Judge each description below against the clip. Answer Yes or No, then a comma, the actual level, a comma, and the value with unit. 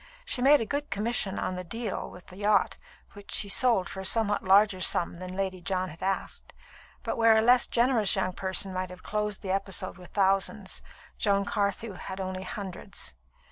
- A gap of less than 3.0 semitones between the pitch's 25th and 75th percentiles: Yes, narrow, 2.5 semitones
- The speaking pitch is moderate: No, high, 195 Hz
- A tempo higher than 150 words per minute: Yes, average, 190 wpm